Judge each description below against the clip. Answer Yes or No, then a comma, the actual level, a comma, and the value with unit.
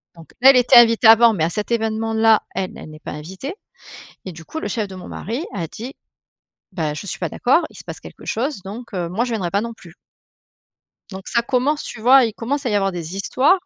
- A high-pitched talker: Yes, high, 220 Hz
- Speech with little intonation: No, average, 4.7 semitones